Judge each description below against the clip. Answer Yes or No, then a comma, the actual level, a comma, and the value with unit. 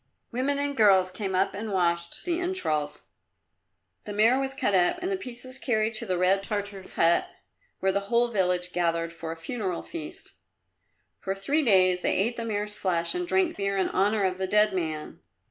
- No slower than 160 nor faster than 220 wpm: Yes, average, 190 wpm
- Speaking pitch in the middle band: No, high, 200 Hz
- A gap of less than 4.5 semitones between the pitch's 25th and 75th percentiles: No, average, 4.8 semitones